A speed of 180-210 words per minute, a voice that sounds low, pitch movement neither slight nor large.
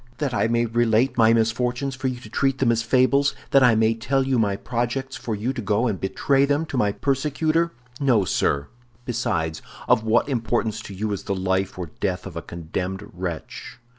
Yes: average, 200 wpm; low, 115 Hz; average, 4.5 semitones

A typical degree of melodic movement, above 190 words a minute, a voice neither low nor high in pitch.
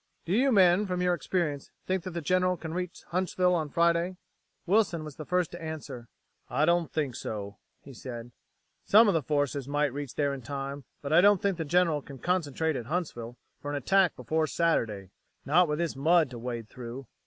Yes: average, 4.6 semitones; average, 200 wpm; medium, 155 Hz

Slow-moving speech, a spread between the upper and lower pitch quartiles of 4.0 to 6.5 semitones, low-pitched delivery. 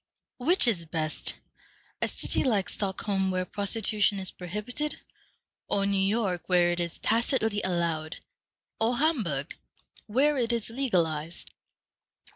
No: slow, 120 wpm; average, 4.9 semitones; high, 200 Hz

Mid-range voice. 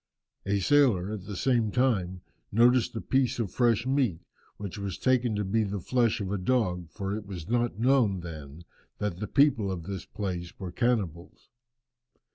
No: low, 105 Hz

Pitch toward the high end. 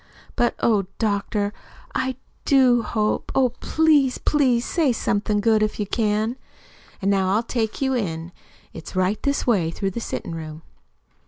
Yes: high, 215 Hz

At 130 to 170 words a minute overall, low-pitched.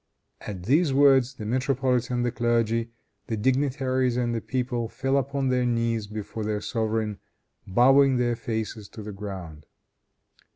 Yes: average, 140 wpm; low, 120 Hz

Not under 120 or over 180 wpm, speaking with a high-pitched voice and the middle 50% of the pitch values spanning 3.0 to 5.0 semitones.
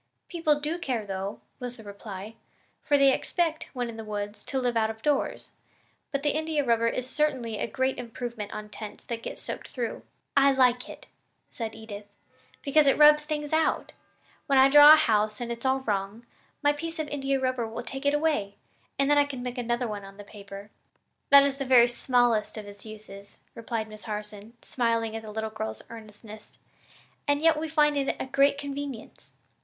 No: average, 195 wpm; high, 245 Hz; average, 4.7 semitones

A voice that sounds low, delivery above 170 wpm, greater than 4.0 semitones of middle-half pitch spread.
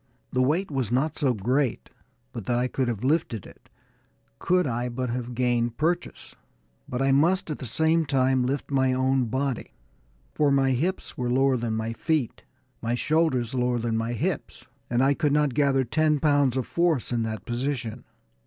No: low, 130 Hz; average, 180 wpm; average, 3.2 semitones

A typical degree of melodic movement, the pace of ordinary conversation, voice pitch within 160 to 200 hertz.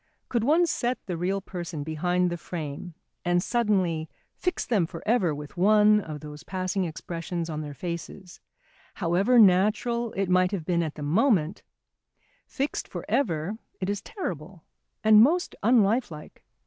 Yes: average, 4.5 semitones; average, 150 wpm; medium, 185 Hz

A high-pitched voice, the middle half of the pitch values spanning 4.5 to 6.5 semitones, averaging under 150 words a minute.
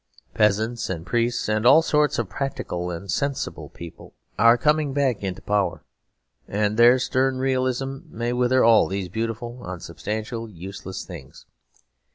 No: low, 115 Hz; average, 4.8 semitones; average, 140 wpm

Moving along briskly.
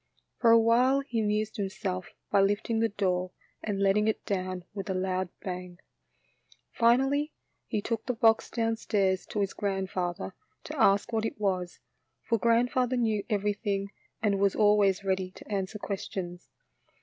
No: average, 155 wpm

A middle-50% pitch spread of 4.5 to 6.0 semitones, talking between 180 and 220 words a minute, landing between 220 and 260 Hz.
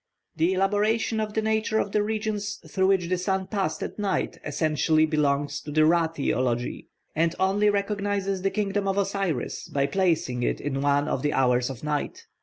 No: wide, 5.5 semitones; average, 185 wpm; medium, 185 Hz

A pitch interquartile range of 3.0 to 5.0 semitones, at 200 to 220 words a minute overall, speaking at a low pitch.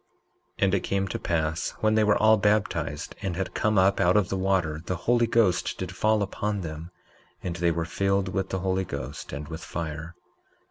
Yes: average, 3.3 semitones; fast, 205 wpm; very low, 95 Hz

